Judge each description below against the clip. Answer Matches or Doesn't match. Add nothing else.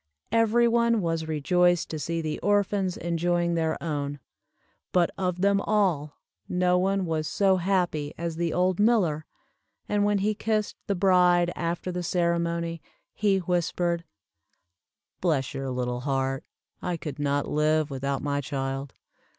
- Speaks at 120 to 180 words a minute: Matches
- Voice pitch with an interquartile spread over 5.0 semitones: Doesn't match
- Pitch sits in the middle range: Matches